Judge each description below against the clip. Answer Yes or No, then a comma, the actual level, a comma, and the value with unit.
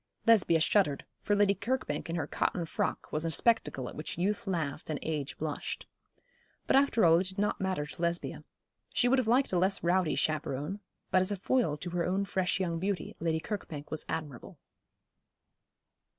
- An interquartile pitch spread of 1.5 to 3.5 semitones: No, average, 4.4 semitones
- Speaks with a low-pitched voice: No, medium, 180 Hz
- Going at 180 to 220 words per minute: Yes, average, 185 wpm